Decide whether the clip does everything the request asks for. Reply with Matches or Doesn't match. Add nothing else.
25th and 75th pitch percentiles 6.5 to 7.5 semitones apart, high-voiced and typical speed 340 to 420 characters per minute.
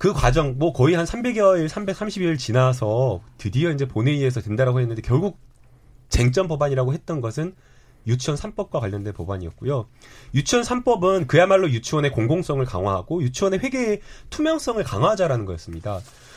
Doesn't match